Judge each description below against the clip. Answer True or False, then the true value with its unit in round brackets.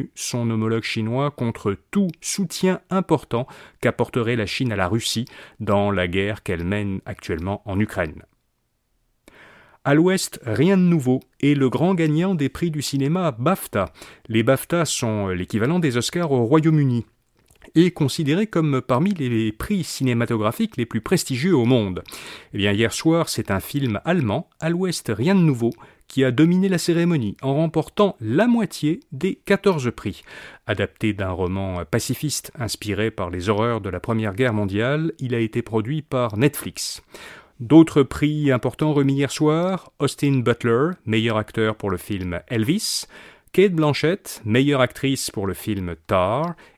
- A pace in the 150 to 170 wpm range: True (155 wpm)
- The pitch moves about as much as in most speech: False (6.3 semitones)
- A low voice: True (130 Hz)